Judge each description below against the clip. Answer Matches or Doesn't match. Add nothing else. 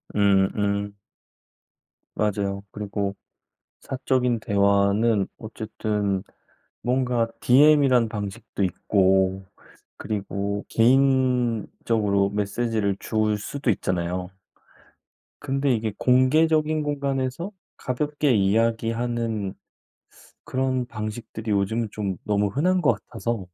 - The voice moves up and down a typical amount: Matches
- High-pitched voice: Doesn't match